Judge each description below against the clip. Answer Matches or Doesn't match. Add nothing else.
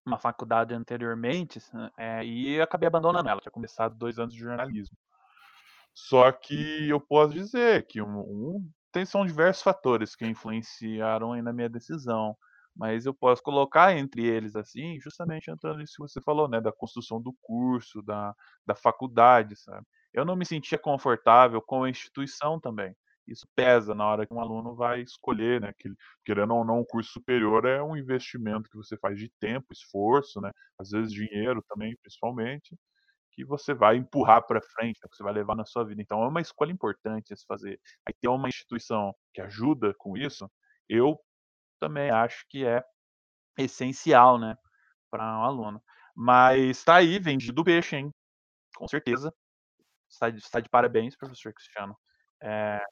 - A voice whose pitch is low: Matches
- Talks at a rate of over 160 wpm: Matches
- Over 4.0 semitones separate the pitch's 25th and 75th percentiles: Matches